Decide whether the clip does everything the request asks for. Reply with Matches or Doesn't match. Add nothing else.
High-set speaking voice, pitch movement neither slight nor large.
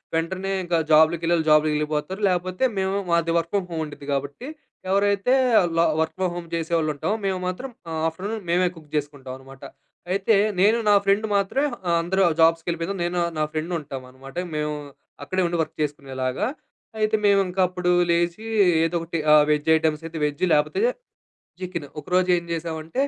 Doesn't match